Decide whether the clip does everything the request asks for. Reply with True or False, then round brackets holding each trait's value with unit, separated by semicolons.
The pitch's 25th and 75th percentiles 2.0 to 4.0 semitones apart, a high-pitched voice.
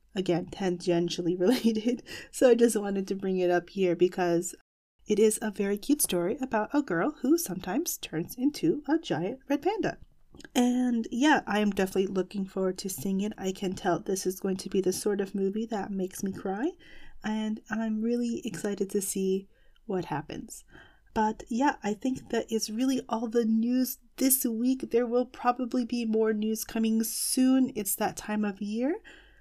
False (4.5 semitones; 220 Hz)